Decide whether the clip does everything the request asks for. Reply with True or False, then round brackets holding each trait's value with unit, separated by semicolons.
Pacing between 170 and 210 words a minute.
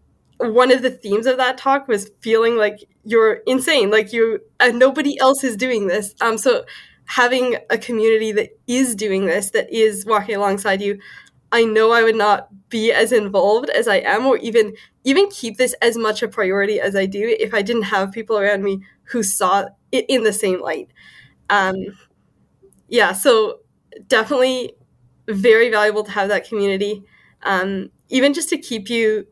True (180 wpm)